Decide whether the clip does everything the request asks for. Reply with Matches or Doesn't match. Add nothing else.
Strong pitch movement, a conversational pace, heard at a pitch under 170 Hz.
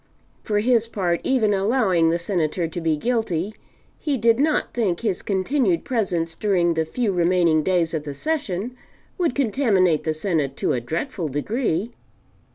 Doesn't match